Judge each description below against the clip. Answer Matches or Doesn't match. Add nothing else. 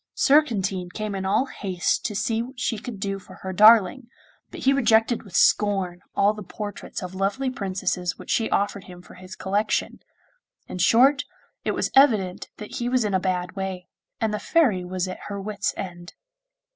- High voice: Matches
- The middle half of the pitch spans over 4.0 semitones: Doesn't match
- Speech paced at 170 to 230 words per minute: Matches